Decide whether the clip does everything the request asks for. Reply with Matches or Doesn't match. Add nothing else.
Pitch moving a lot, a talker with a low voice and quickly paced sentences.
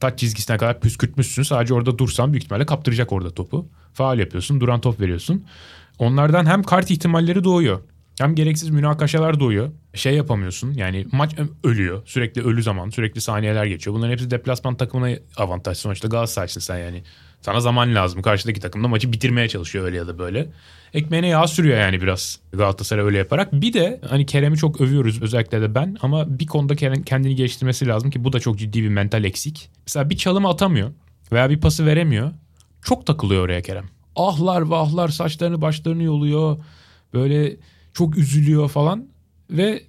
Matches